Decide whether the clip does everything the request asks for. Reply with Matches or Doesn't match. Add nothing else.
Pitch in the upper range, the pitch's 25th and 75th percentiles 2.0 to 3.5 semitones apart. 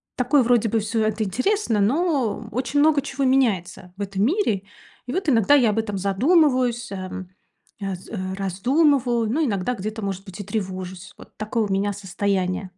Doesn't match